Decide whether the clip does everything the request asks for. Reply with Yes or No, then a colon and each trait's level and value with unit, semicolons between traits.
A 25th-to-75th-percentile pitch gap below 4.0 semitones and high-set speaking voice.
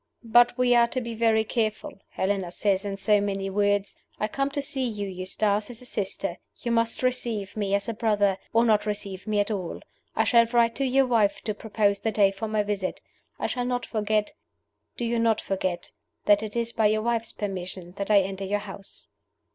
Yes: average, 2.7 semitones; high, 210 Hz